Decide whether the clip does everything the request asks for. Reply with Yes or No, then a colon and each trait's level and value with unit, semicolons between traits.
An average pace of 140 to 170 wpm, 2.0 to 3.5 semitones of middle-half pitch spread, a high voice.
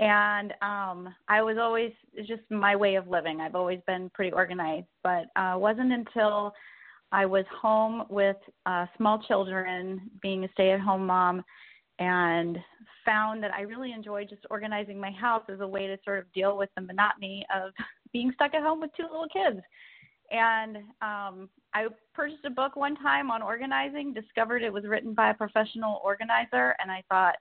No: average, 185 wpm; average, 2.9 semitones; high, 205 Hz